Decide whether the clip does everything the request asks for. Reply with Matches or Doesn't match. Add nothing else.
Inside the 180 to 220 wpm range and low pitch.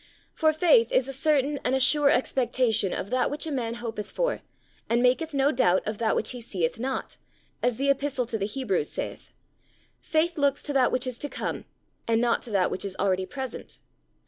Doesn't match